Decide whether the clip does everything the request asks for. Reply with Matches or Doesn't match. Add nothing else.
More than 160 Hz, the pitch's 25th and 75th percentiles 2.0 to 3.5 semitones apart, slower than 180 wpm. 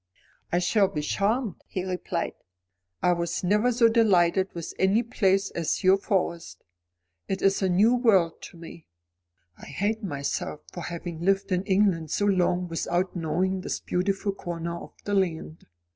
Matches